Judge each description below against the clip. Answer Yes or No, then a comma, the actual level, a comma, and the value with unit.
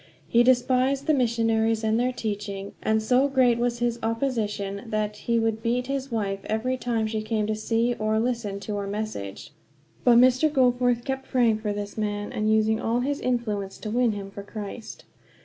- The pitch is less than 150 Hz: No, high, 225 Hz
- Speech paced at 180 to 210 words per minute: Yes, average, 190 wpm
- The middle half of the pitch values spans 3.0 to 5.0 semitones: No, narrow, 2.6 semitones